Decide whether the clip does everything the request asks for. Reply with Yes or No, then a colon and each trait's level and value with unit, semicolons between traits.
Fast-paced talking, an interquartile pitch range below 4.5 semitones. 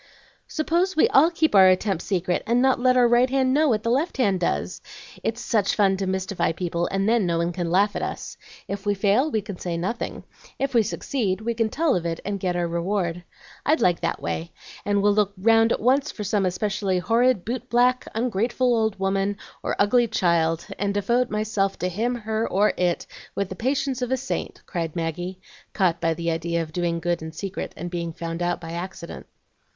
No: fast, 210 wpm; average, 5.1 semitones